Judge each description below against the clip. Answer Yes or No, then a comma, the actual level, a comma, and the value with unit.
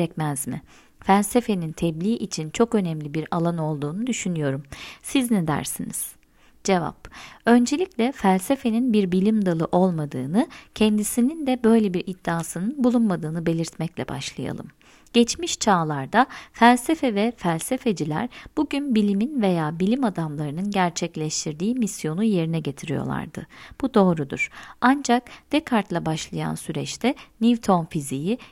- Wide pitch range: Yes, wide, 6.4 semitones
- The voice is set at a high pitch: Yes, high, 200 Hz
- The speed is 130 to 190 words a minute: No, average, 105 wpm